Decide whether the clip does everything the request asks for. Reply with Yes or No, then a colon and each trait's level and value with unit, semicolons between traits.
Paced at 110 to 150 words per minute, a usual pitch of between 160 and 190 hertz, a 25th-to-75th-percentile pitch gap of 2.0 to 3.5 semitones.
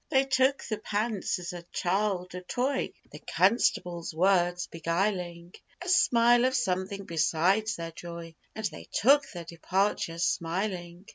No: average, 140 wpm; medium, 185 Hz; average, 4.2 semitones